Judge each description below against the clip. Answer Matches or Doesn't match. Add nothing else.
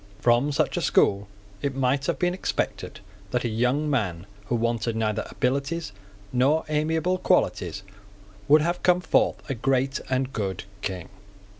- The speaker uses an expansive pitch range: Doesn't match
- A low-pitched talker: Matches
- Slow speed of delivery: Doesn't match